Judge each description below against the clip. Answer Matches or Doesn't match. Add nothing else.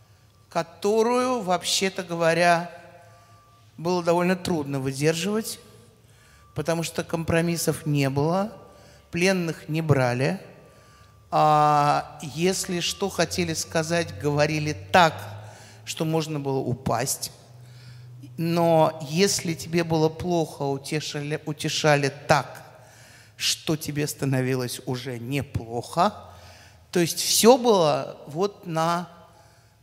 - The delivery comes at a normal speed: Doesn't match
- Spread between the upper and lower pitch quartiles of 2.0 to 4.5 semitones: Doesn't match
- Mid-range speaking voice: Matches